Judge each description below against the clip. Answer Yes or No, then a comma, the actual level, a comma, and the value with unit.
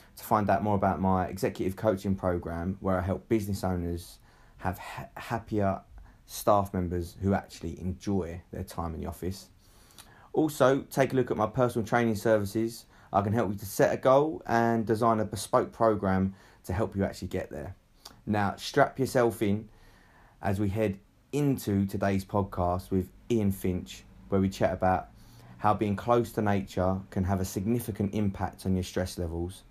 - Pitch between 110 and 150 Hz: No, low, 100 Hz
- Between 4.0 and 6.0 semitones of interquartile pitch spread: No, average, 3.3 semitones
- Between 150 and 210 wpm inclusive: Yes, average, 175 wpm